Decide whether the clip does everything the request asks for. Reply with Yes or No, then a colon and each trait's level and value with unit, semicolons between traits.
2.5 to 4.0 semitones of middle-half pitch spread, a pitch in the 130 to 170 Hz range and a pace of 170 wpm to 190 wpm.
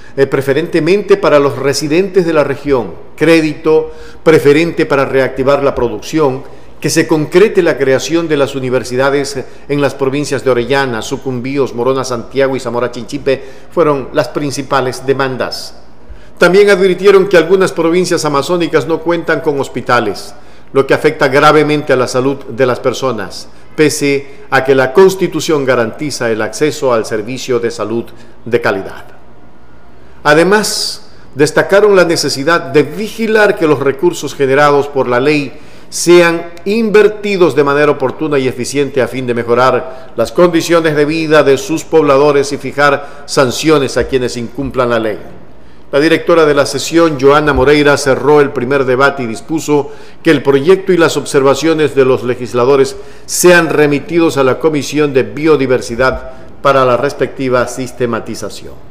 No: average, 3.6 semitones; medium, 140 Hz; average, 145 wpm